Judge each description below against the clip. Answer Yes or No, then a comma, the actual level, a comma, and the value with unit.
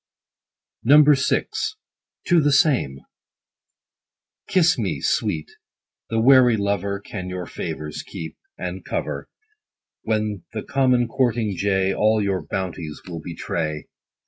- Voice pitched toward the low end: Yes, low, 100 Hz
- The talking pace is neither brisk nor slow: No, slow, 115 wpm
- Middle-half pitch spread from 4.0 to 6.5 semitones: Yes, wide, 5.5 semitones